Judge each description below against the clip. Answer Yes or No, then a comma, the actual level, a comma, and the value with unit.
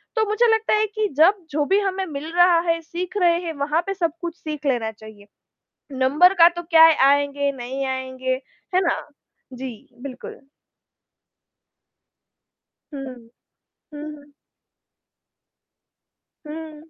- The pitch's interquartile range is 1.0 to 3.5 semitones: No, average, 5.0 semitones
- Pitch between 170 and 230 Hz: No, very high, 310 Hz